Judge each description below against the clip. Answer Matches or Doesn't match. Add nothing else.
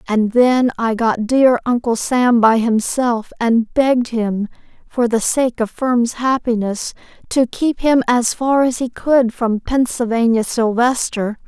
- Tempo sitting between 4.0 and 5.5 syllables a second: Doesn't match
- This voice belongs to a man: Doesn't match